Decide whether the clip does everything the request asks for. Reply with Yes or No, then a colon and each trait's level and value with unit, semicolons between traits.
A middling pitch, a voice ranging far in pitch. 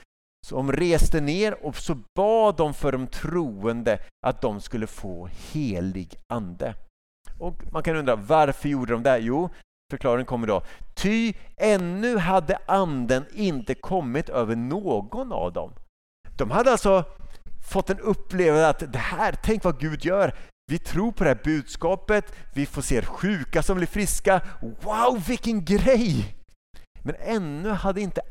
Yes: medium, 170 Hz; wide, 6.6 semitones